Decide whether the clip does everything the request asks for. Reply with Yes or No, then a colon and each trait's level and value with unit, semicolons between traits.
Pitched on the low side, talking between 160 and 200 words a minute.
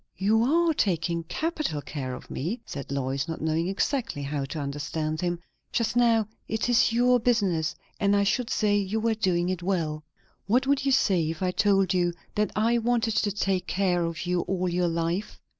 No: high, 190 Hz; average, 190 wpm